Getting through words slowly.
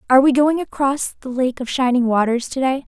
No: fast, 205 wpm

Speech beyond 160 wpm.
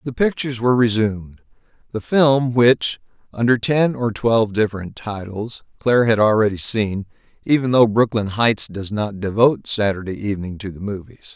No: average, 155 wpm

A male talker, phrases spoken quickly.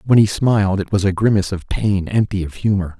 Yes: male; fast, 240 wpm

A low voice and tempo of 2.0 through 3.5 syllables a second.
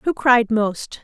No: high, 240 Hz; 3.0 syllables/s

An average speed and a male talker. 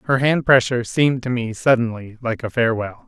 Yes: average, 195 wpm; male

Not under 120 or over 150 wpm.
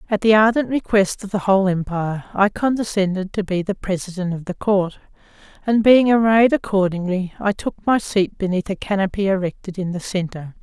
No: average, 180 wpm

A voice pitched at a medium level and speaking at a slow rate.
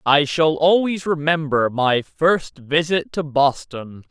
Yes: medium, 150 Hz; slow, 130 wpm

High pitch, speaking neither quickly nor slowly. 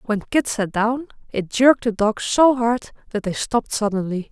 Yes: high, 225 Hz; average, 195 wpm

